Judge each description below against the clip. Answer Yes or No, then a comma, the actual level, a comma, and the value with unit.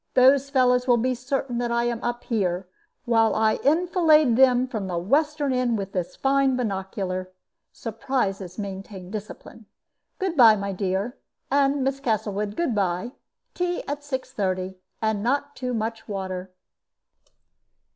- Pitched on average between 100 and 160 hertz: No, high, 235 Hz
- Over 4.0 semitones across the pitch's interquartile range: Yes, average, 5.3 semitones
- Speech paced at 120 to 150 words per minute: Yes, average, 140 wpm